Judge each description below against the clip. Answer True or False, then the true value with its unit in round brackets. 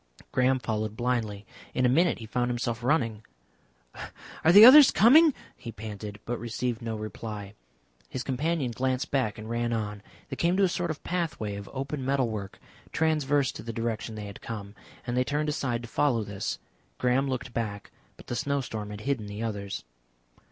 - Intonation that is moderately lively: True (4.4 semitones)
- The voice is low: True (120 Hz)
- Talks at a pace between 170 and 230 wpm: True (180 wpm)